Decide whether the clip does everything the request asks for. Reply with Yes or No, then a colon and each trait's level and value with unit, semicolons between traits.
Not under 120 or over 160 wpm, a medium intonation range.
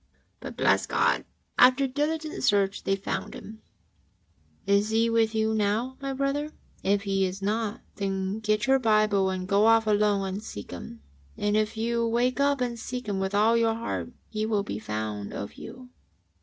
No: average, 180 wpm; average, 3.0 semitones